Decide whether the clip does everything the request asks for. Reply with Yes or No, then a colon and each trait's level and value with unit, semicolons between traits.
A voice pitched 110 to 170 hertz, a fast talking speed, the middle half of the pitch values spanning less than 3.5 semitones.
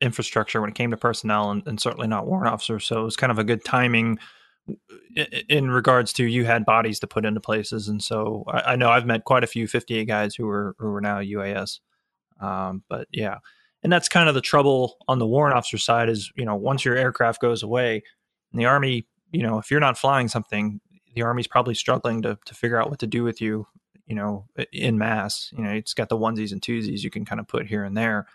Yes: low, 115 Hz; fast, 240 wpm; narrow, 2.6 semitones